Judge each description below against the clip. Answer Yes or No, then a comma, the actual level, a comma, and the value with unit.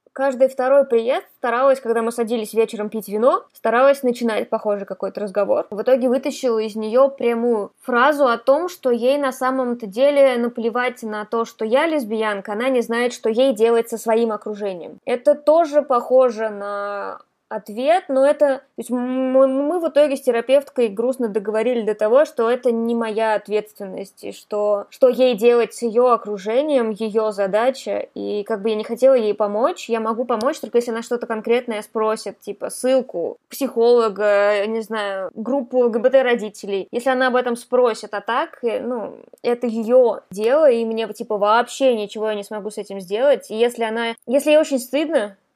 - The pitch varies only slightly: No, average, 3.2 semitones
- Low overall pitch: No, high, 235 Hz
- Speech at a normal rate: No, fast, 175 wpm